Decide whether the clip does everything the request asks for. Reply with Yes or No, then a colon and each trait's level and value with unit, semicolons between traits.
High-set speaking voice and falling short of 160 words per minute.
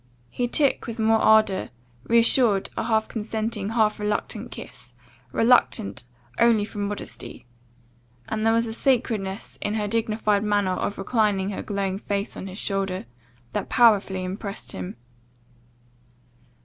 Yes: high, 210 Hz; slow, 135 wpm